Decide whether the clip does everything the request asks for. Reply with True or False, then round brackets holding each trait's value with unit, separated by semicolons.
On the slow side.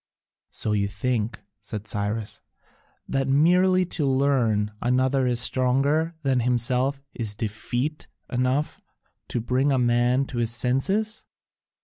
True (120 wpm)